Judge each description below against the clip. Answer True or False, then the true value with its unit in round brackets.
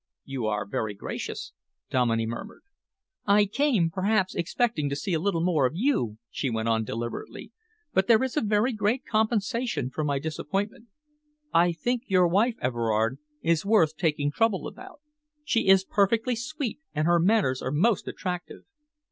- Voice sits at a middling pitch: True (180 Hz)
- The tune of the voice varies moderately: False (7.9 semitones)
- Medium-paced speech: True (160 wpm)